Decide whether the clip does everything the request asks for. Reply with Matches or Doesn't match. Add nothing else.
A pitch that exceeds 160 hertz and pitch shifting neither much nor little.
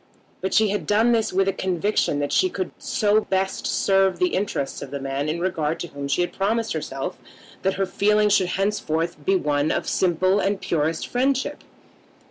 Matches